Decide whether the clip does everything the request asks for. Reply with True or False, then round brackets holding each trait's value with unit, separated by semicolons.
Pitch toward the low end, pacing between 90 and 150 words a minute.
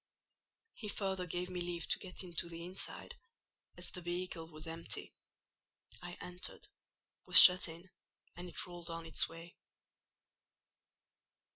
False (175 Hz; 135 wpm)